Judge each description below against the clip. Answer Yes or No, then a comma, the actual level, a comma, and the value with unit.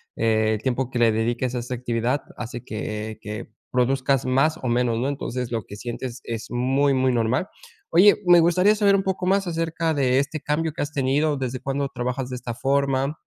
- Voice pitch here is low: Yes, low, 130 Hz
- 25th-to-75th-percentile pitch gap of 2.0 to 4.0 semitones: Yes, average, 3.5 semitones